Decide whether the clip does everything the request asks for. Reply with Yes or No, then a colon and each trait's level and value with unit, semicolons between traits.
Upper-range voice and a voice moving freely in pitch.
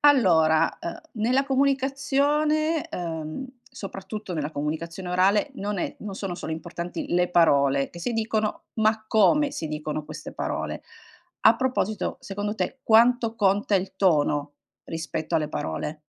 Yes: high, 195 Hz; wide, 6.3 semitones